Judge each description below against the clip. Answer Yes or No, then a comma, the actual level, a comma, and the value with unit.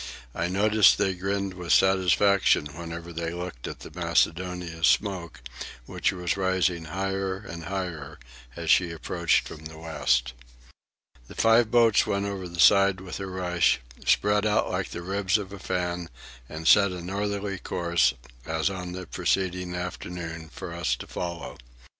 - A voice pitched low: Yes, very low, 90 Hz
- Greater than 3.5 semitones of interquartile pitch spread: No, narrow, 2.4 semitones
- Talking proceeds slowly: No, average, 155 wpm